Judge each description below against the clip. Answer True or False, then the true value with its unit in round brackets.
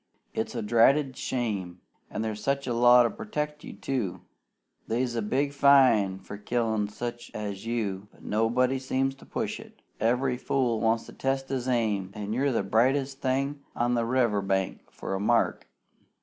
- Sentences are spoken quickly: False (170 wpm)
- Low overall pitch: True (120 Hz)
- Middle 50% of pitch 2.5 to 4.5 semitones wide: True (3.8 semitones)